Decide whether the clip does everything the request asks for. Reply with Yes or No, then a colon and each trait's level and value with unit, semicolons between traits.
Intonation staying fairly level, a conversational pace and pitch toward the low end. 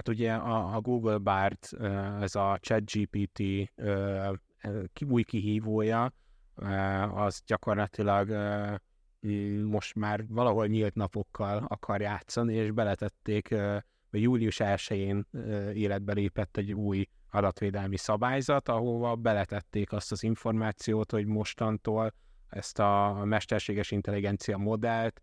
No: narrow, 1.6 semitones; slow, 100 wpm; low, 105 Hz